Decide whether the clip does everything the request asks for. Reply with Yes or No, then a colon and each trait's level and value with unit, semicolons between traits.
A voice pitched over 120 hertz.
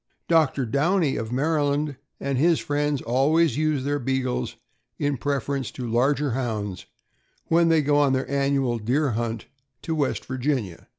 Yes: medium, 140 Hz